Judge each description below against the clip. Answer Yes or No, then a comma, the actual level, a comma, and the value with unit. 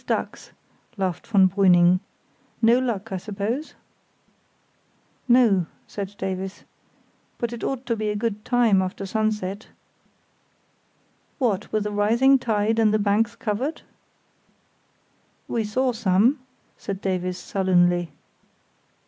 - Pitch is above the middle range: Yes, high, 210 Hz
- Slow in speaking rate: Yes, slow, 115 wpm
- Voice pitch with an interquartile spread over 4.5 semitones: No, average, 3.3 semitones